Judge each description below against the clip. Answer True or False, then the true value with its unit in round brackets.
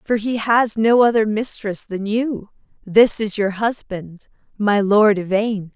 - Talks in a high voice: True (210 Hz)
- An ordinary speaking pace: True (155 wpm)